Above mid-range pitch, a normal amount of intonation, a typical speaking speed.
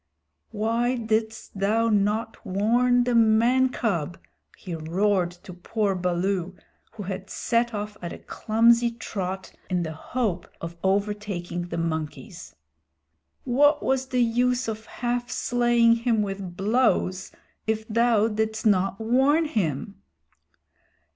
No: high, 220 Hz; average, 3.8 semitones; slow, 125 wpm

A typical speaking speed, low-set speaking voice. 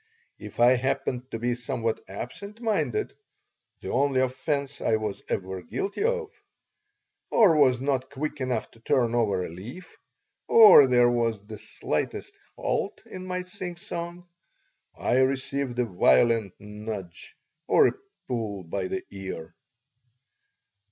No: slow, 130 wpm; low, 125 Hz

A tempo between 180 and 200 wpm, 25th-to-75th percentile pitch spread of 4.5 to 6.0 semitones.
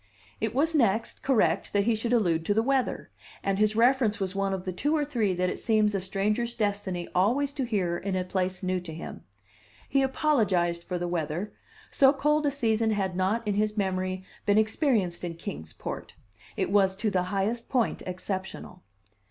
No: average, 195 wpm; average, 4.0 semitones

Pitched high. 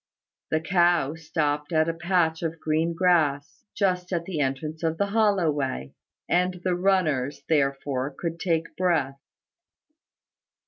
No: medium, 160 Hz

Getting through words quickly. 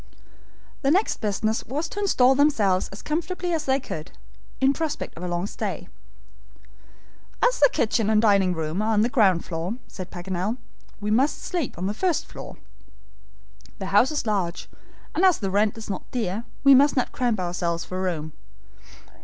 No: average, 175 wpm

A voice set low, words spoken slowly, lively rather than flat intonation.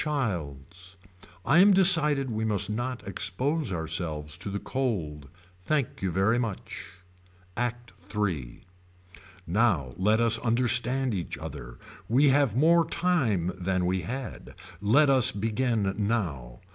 Yes: low, 110 Hz; slow, 125 wpm; wide, 6.2 semitones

